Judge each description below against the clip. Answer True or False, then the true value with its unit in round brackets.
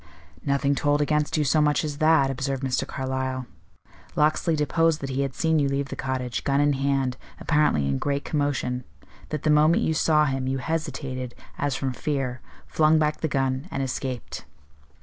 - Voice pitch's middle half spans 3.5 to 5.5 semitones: False (2.4 semitones)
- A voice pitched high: False (140 Hz)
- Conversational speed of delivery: True (180 wpm)